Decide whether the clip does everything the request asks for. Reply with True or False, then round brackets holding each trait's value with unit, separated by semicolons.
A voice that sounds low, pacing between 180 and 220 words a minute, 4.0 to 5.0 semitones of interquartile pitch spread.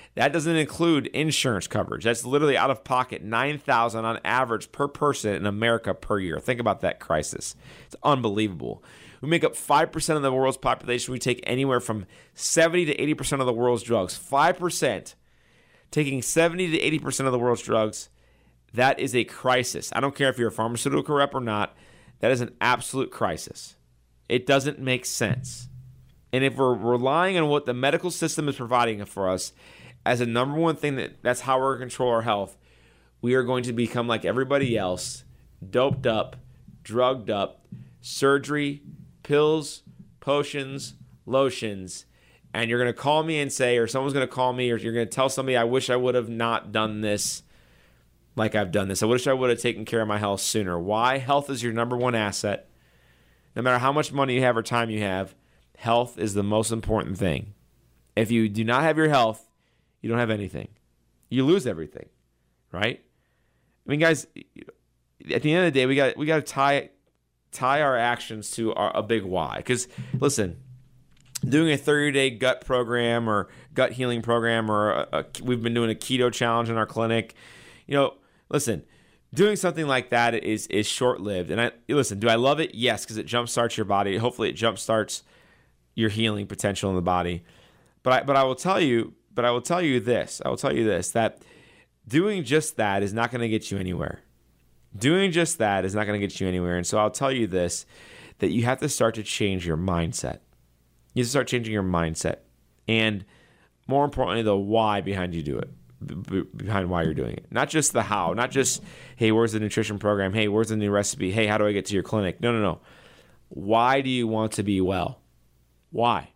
True (120 Hz; 200 wpm; 4.5 semitones)